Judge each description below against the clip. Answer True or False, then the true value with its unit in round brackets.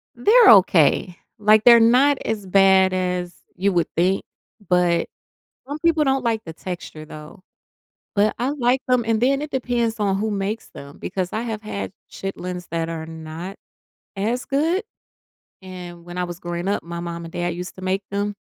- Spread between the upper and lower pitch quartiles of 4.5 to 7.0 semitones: True (4.8 semitones)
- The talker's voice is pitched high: True (195 Hz)